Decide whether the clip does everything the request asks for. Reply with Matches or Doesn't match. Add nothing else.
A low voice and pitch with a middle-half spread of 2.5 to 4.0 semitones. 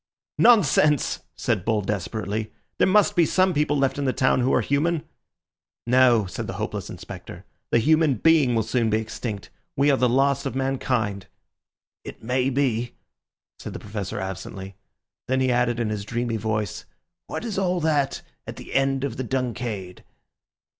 Doesn't match